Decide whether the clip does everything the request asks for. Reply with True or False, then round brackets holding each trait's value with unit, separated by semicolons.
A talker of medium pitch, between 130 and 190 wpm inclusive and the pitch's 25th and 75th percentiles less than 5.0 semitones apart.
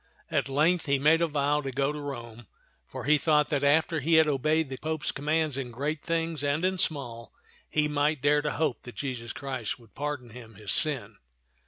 False (145 Hz; 205 wpm; 3.1 semitones)